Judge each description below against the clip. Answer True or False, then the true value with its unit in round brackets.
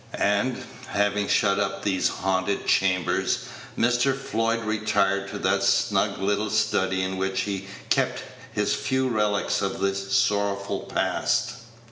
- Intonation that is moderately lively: False (1.8 semitones)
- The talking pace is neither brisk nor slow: False (130 wpm)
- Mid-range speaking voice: False (100 Hz)